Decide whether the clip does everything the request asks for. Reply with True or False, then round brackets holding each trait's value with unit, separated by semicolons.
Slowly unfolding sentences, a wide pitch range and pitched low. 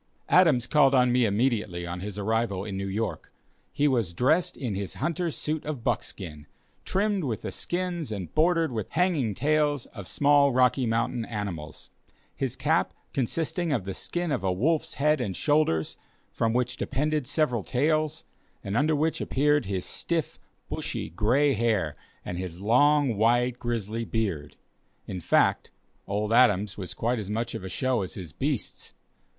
False (165 wpm; 6.5 semitones; 120 Hz)